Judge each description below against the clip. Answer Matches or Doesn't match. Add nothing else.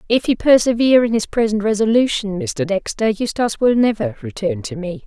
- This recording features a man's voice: Doesn't match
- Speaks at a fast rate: Doesn't match